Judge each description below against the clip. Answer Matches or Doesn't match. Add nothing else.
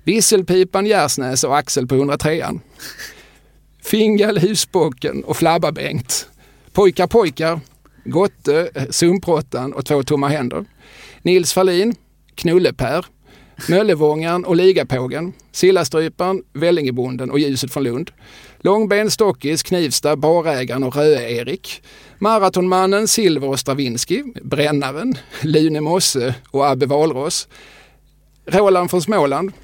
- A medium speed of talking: Doesn't match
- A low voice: Doesn't match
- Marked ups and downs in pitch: Doesn't match